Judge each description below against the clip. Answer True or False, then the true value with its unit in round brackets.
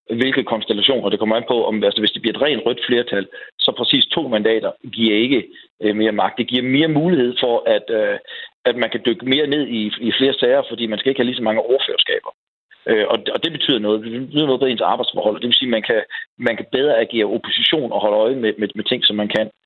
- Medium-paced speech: False (240 wpm)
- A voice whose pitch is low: True (125 Hz)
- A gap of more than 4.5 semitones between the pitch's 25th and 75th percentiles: True (5.5 semitones)